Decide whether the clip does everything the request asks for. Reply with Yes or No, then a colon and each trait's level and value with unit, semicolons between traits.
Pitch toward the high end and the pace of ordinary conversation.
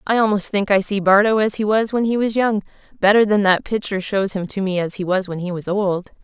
No: high, 200 Hz; fast, 270 wpm